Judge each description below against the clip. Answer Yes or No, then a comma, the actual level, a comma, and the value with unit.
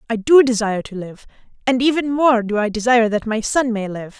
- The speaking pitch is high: Yes, high, 230 Hz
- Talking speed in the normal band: No, fast, 230 wpm